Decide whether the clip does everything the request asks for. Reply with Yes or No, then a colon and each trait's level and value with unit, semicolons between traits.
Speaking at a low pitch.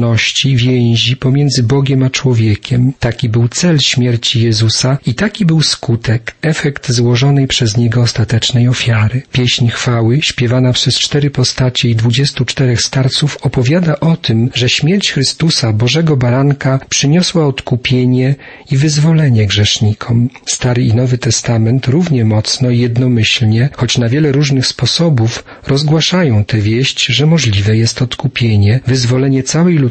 Yes: low, 125 Hz